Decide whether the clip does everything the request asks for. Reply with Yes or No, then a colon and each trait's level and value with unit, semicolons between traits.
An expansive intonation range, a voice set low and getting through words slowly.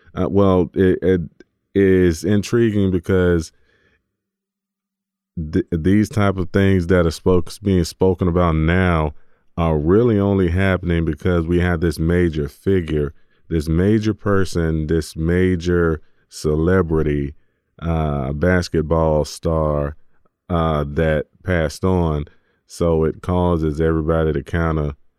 No: average, 2.8 semitones; very low, 85 Hz; slow, 115 wpm